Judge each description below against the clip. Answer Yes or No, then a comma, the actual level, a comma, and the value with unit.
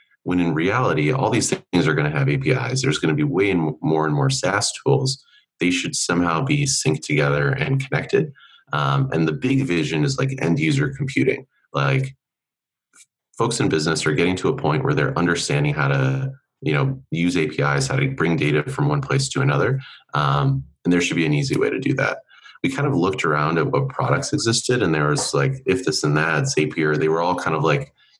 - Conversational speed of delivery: No, fast, 215 wpm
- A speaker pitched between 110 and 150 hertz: Yes, low, 130 Hz